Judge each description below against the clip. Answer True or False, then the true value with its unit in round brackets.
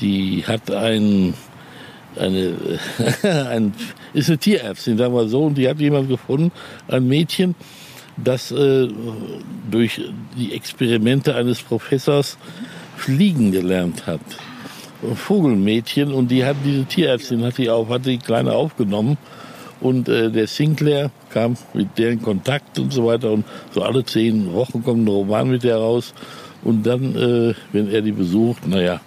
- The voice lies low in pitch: True (120 Hz)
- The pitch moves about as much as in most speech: True (4.0 semitones)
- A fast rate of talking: False (155 wpm)